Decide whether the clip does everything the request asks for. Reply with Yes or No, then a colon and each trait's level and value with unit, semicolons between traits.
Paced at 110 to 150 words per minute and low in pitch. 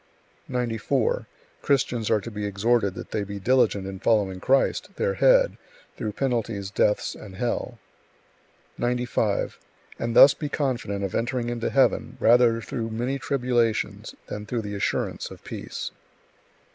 Yes: average, 140 wpm; low, 115 Hz